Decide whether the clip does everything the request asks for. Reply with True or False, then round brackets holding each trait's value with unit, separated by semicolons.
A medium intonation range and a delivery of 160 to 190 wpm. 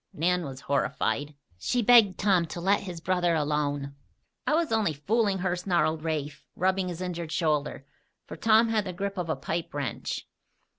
True (4.5 semitones; 170 wpm)